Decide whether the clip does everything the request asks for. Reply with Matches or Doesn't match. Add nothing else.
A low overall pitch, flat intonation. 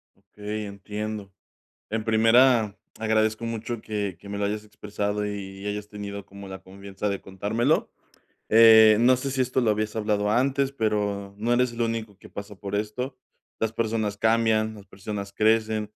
Matches